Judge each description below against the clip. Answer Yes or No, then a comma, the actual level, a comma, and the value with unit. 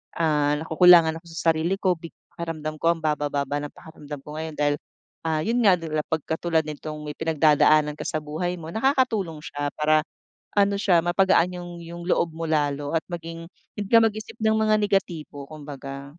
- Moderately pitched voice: Yes, medium, 160 Hz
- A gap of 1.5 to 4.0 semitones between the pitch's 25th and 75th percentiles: Yes, average, 2.8 semitones